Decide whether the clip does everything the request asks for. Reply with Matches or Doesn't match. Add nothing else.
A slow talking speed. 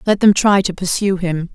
Doesn't match